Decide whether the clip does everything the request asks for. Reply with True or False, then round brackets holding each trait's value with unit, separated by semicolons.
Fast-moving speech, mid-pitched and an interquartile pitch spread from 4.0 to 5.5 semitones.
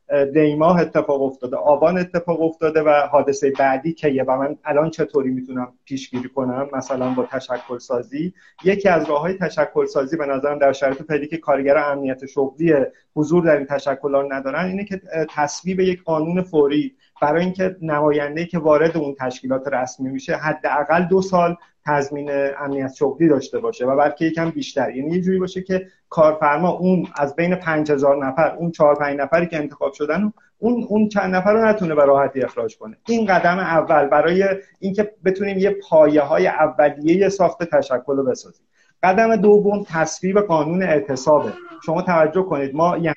True (170 wpm; 155 Hz; 4.3 semitones)